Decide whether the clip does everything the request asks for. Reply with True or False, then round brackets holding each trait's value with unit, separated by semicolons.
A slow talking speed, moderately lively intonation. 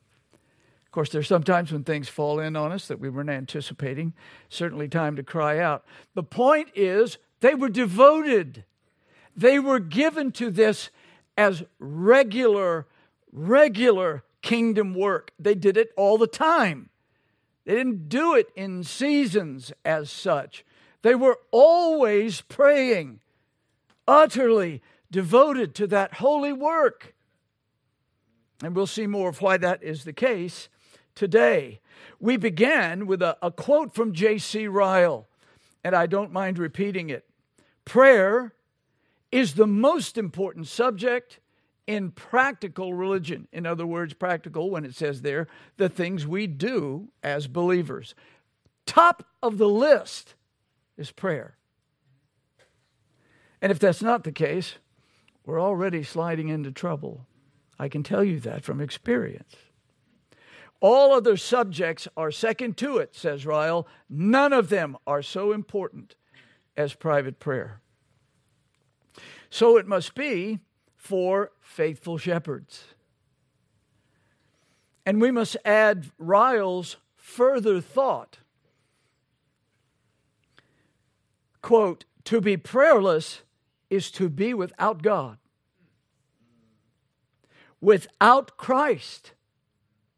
False (115 wpm; 7.3 semitones)